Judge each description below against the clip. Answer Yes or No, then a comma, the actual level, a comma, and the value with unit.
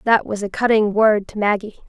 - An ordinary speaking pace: No, fast, 225 wpm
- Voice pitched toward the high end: Yes, high, 210 Hz